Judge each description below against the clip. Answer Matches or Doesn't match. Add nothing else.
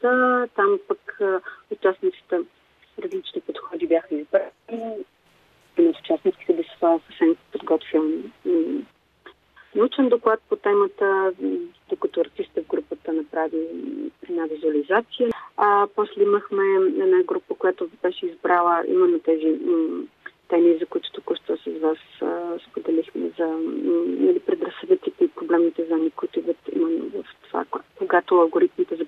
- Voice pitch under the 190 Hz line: Doesn't match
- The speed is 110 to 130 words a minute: Matches